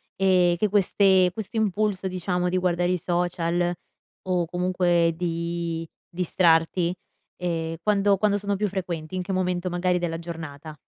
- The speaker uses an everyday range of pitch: No, narrow, 1.8 semitones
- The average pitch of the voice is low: No, medium, 180 Hz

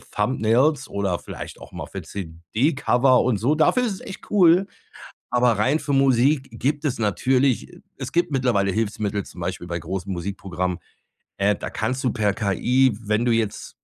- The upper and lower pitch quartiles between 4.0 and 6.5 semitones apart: Yes, average, 5.2 semitones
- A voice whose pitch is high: No, low, 120 Hz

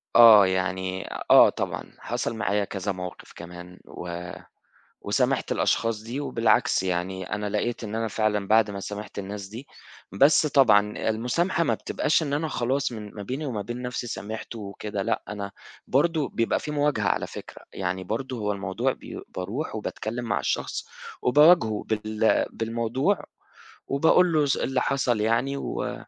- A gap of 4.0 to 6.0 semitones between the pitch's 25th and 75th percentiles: Yes, average, 4.5 semitones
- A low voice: Yes, low, 110 Hz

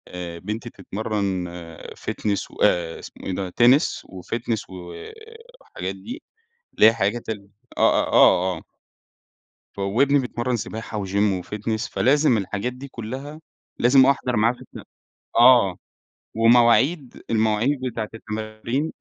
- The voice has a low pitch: Yes, low, 110 Hz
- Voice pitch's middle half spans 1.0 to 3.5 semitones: No, average, 4.1 semitones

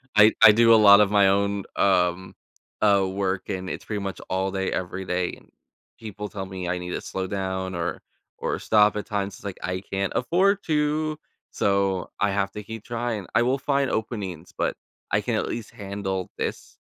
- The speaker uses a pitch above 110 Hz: No, low, 100 Hz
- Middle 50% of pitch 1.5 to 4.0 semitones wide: Yes, narrow, 2.5 semitones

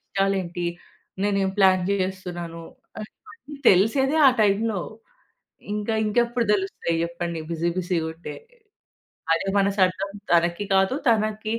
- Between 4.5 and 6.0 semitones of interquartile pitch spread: No, average, 3.4 semitones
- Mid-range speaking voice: No, high, 195 Hz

